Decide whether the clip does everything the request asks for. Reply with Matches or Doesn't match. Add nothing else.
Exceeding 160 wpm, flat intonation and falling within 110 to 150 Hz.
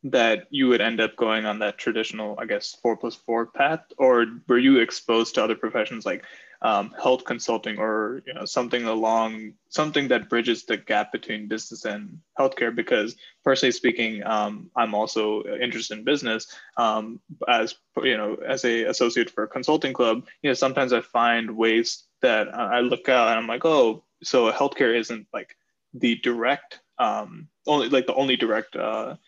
Matches